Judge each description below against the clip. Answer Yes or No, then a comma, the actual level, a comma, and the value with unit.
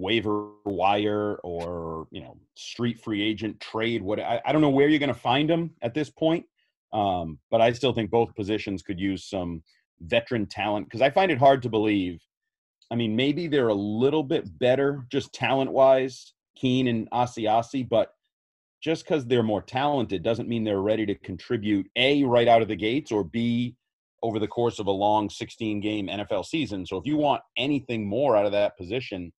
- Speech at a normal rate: Yes, average, 195 wpm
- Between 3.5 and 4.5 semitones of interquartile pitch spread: Yes, average, 4.2 semitones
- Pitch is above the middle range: No, low, 115 Hz